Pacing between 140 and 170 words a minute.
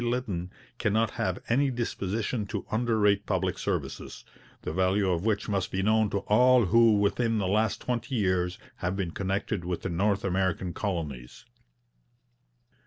Yes: average, 150 wpm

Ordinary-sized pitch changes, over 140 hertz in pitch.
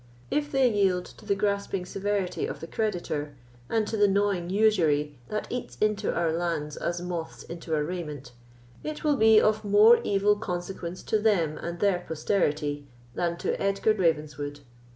Yes: average, 4.2 semitones; medium, 185 Hz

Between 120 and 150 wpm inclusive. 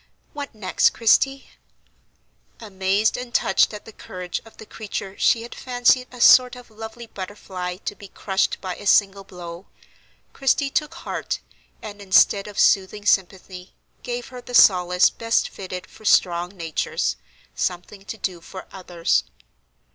Yes: average, 145 wpm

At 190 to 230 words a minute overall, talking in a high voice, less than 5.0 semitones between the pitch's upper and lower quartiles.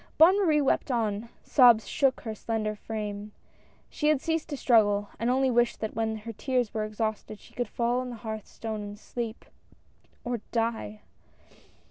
No: average, 170 wpm; high, 230 Hz; average, 2.8 semitones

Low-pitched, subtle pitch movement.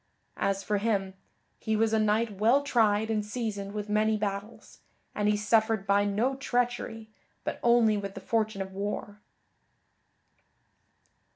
No: high, 215 Hz; narrow, 1.8 semitones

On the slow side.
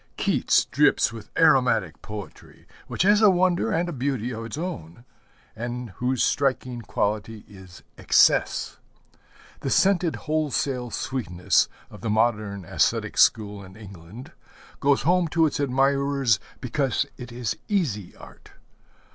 Yes: slow, 130 wpm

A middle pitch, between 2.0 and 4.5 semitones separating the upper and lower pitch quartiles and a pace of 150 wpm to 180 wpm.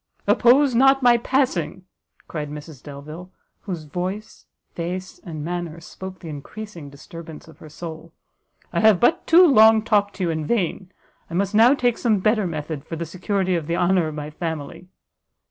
No: medium, 180 Hz; average, 5.3 semitones; average, 175 wpm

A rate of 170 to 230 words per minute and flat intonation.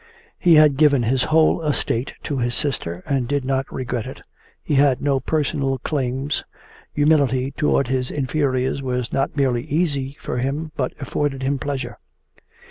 No: average, 155 wpm; narrow, 2.1 semitones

